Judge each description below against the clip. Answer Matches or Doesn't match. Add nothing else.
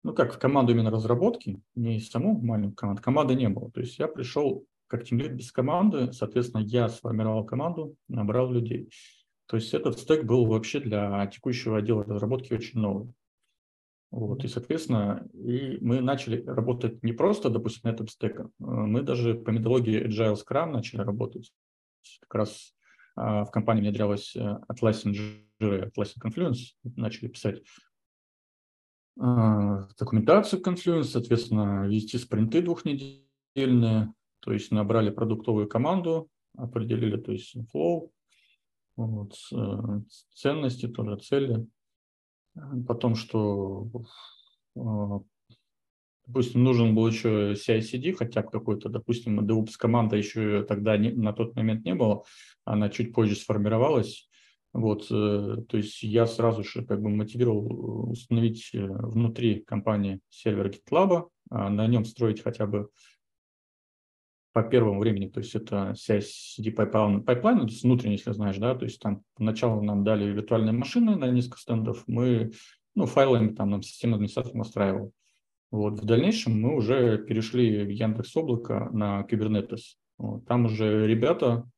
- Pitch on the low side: Matches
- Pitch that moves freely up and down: Doesn't match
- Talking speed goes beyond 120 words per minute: Matches